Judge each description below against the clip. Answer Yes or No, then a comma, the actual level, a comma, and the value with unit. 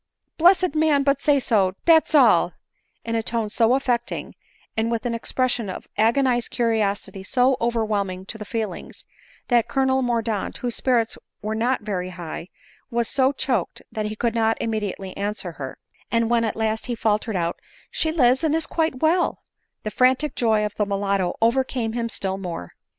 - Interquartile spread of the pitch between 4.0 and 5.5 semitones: No, average, 3.5 semitones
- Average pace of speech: Yes, average, 180 wpm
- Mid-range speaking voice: No, high, 230 Hz